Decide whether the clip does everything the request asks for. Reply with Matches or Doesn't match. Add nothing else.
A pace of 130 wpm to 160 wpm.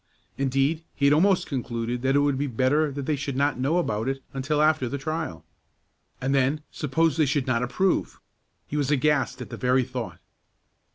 Doesn't match